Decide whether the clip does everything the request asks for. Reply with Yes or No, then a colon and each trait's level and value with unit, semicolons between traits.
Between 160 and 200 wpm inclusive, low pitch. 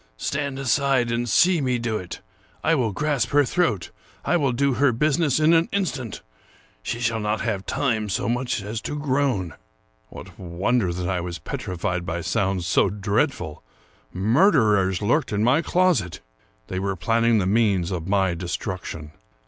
Yes: average, 165 wpm; low, 110 Hz